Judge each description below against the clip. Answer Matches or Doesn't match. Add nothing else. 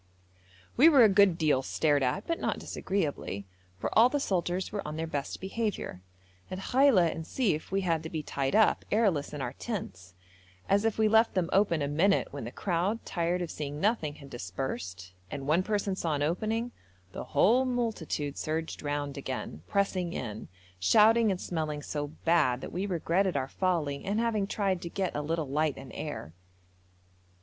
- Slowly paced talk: Doesn't match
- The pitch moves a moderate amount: Doesn't match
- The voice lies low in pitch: Doesn't match